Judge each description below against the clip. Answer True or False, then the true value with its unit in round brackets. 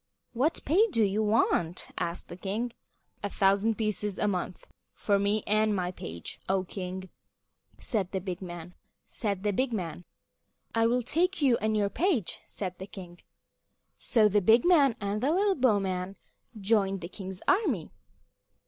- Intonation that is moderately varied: True (3.7 semitones)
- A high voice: True (205 Hz)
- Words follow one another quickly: False (150 wpm)